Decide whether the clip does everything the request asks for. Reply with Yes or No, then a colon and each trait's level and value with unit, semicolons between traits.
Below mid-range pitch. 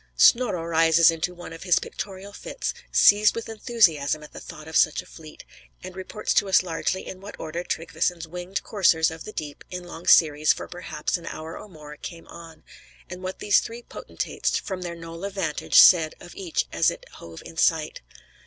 No: medium, 170 Hz